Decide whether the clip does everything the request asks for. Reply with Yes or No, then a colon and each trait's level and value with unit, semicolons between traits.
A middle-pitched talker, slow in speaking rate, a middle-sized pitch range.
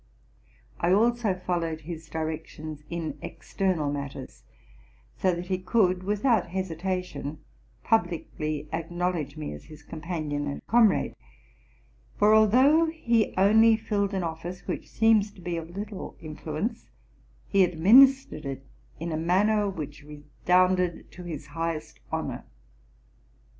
Yes: medium, 180 Hz; slow, 125 wpm; average, 4.5 semitones